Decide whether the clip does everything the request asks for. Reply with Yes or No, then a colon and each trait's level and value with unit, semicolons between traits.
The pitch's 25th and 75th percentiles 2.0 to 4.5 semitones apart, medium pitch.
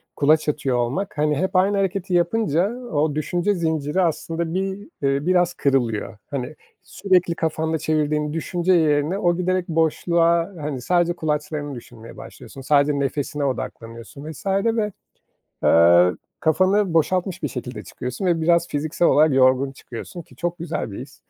Yes: average, 3.9 semitones; medium, 160 Hz